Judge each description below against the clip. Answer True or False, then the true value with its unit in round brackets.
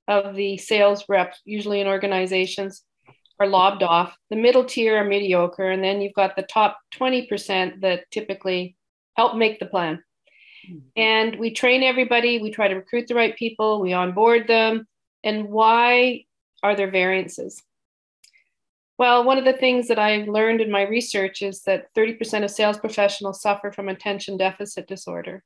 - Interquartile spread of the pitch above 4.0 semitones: False (2.9 semitones)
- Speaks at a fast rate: False (165 wpm)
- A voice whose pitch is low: False (205 Hz)